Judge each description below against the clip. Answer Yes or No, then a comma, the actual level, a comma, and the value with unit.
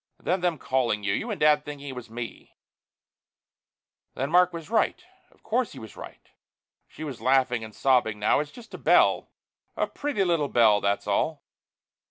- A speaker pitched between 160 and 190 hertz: No, medium, 140 Hz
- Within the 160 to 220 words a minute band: Yes, average, 190 wpm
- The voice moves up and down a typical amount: No, wide, 6.7 semitones